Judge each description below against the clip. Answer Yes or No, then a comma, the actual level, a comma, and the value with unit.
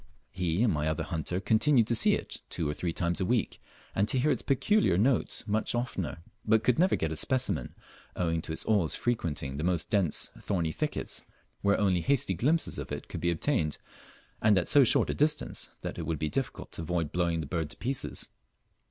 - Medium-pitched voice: No, very low, 90 Hz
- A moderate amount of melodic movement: No, wide, 6.5 semitones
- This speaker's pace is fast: Yes, fast, 210 wpm